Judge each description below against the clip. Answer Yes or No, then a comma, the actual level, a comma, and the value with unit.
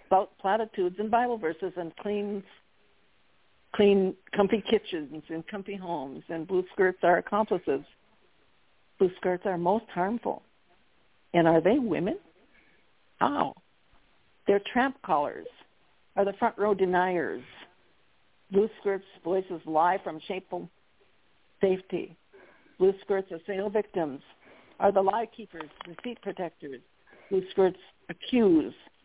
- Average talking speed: No, slow, 120 wpm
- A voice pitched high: Yes, high, 195 Hz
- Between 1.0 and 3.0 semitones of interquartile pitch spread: Yes, narrow, 2.6 semitones